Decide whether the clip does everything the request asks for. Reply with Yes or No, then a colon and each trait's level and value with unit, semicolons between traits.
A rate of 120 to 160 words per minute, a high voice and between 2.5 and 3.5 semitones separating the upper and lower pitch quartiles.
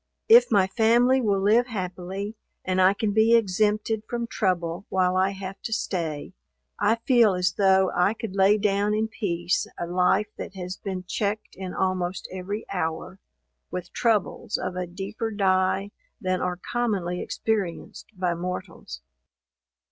Yes: average, 150 wpm; high, 195 Hz; average, 2.8 semitones